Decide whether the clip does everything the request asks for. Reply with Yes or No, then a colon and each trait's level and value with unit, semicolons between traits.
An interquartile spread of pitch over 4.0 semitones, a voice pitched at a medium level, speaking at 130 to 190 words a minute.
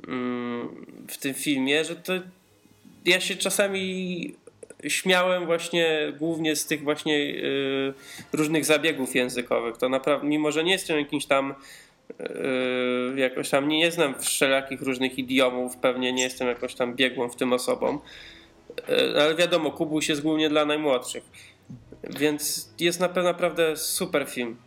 Yes: average, 4.5 semitones; medium, 150 Hz; average, 140 wpm